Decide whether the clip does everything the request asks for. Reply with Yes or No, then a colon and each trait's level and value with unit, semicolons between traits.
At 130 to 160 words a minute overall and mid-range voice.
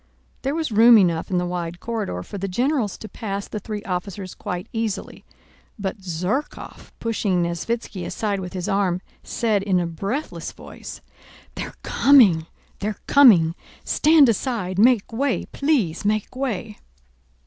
No: average, 145 wpm; high, 205 Hz